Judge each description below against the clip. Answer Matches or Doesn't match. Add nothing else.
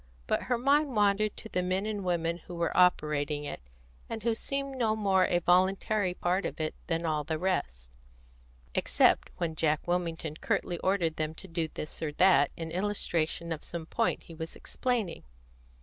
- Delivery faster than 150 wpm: Matches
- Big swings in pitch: Doesn't match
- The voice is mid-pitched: Matches